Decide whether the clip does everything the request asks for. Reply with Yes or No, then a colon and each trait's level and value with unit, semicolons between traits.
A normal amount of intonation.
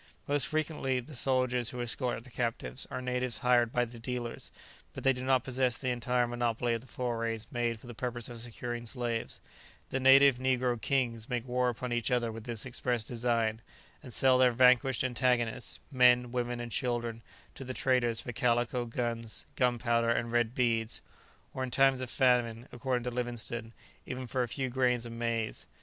No: narrow, 1.4 semitones